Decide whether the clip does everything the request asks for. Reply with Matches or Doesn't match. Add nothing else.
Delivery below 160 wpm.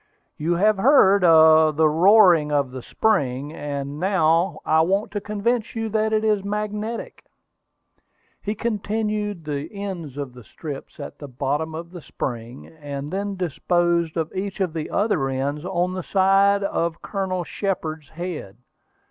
Matches